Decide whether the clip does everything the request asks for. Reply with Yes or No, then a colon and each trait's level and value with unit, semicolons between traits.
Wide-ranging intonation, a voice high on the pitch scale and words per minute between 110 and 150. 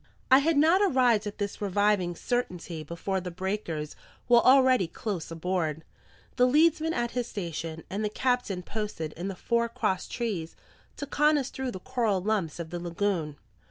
No: wide, 6.2 semitones; high, 205 Hz; average, 170 wpm